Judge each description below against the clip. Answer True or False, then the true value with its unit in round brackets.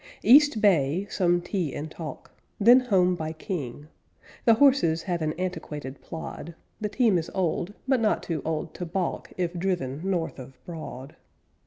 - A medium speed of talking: True (160 wpm)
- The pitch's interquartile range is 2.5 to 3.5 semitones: False (4.1 semitones)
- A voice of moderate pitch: True (175 Hz)